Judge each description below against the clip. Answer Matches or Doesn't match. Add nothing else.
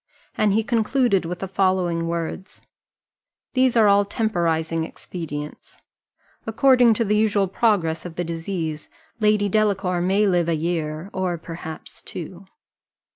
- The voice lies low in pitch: Doesn't match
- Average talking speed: Doesn't match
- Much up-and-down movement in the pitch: Doesn't match